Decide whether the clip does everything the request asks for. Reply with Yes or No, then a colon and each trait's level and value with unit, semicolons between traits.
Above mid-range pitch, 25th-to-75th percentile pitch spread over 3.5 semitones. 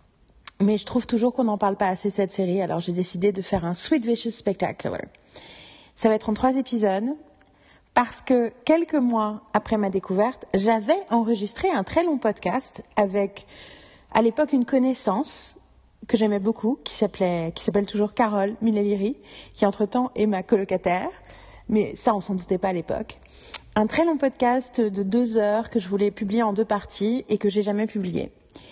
No: high, 215 Hz; average, 3.2 semitones